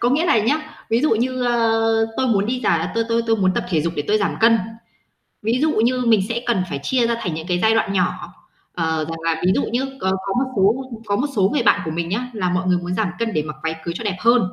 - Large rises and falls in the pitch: No, average, 4.7 semitones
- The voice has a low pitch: No, high, 215 Hz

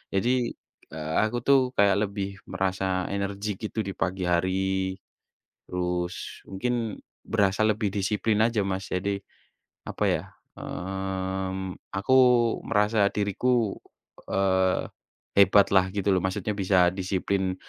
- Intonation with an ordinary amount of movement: No, narrow, 1.5 semitones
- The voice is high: No, very low, 95 Hz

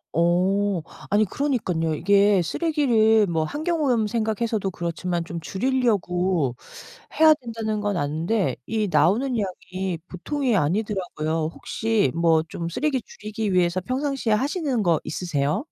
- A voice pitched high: Yes, high, 200 Hz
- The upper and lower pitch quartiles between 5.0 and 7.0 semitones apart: Yes, average, 5.3 semitones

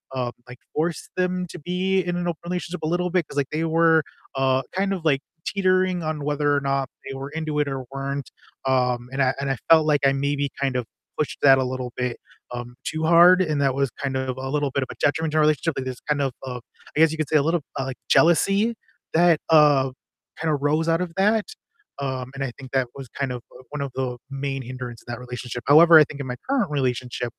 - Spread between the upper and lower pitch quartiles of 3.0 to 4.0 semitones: Yes, average, 3.7 semitones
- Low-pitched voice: No, medium, 145 Hz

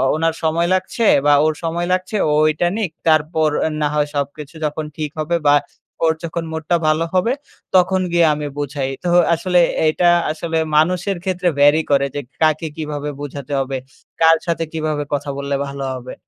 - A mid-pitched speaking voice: Yes, medium, 155 Hz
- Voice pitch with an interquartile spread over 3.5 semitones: No, average, 2.8 semitones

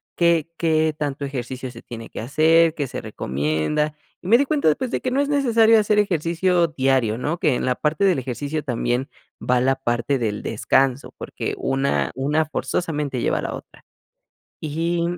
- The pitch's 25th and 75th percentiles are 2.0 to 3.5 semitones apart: No, average, 4.7 semitones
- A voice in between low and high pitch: Yes, medium, 150 Hz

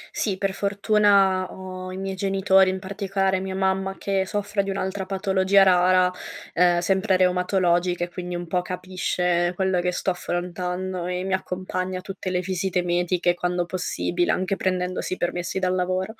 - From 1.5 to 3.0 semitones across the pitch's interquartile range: No, narrow, 1.1 semitones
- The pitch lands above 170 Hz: Yes, medium, 185 Hz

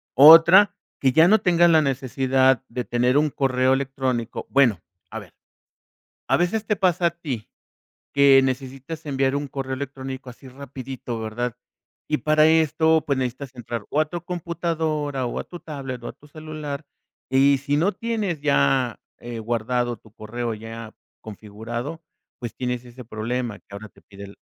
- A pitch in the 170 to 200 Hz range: No, low, 135 Hz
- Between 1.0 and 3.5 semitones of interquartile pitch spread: No, average, 4.1 semitones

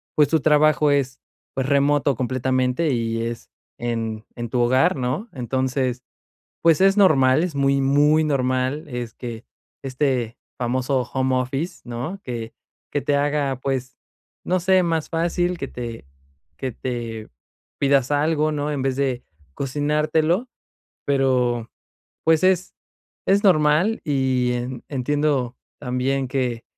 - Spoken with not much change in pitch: No, average, 3.3 semitones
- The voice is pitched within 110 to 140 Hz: Yes, low, 135 Hz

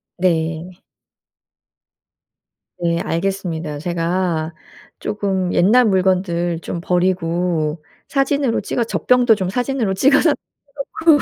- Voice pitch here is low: No, medium, 185 Hz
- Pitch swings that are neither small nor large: Yes, average, 4.1 semitones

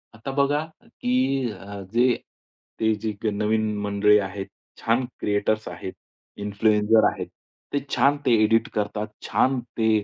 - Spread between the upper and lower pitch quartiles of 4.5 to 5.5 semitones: No, narrow, 2.6 semitones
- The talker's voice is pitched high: No, low, 110 Hz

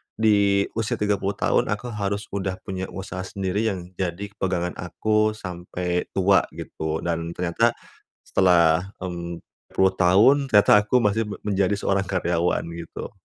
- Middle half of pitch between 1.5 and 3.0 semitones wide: Yes, average, 2.7 semitones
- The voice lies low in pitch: Yes, very low, 95 Hz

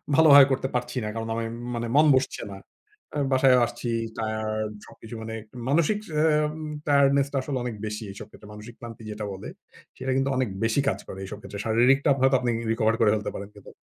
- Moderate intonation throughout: Yes, average, 3.8 semitones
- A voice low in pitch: Yes, low, 120 Hz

